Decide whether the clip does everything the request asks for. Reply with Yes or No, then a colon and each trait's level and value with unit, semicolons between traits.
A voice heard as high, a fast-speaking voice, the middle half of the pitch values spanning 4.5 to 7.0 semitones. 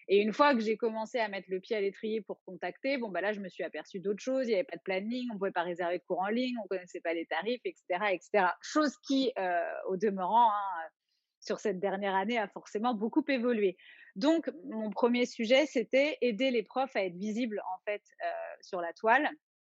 Yes: high, 220 Hz; fast, 235 wpm; average, 5.2 semitones